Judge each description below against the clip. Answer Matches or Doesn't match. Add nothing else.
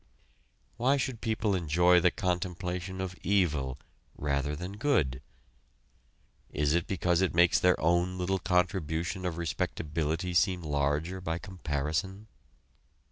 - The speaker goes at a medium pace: Doesn't match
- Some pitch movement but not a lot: Matches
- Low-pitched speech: Matches